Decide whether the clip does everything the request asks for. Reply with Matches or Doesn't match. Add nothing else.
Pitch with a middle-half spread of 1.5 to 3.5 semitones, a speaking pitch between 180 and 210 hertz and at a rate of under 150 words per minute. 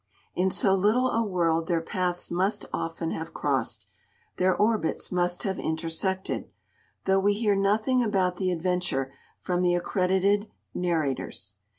Matches